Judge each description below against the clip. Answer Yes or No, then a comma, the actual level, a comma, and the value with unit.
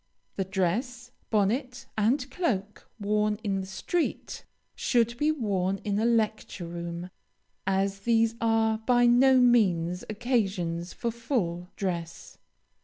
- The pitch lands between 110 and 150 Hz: No, high, 215 Hz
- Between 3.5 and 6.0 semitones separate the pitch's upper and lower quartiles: Yes, average, 4.1 semitones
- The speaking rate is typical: No, slow, 120 wpm